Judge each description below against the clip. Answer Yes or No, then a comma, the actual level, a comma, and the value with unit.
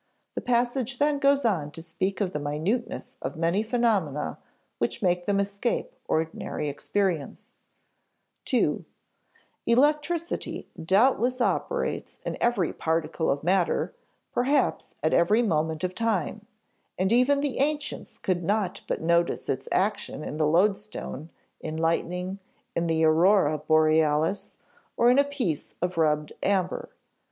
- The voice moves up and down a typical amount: No, wide, 6.8 semitones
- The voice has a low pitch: No, medium, 185 Hz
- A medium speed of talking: No, slow, 130 wpm